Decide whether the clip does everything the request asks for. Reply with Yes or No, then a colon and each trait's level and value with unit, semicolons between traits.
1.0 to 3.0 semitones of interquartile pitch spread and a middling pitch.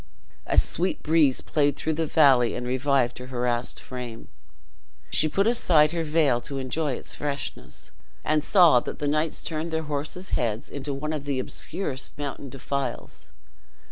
No: average, 3.6 semitones; medium, 145 Hz